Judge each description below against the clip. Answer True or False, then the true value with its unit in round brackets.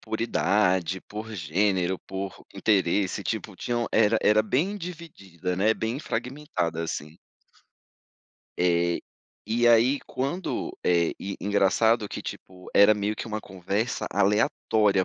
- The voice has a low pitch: True (105 Hz)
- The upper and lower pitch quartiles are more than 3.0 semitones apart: True (3.6 semitones)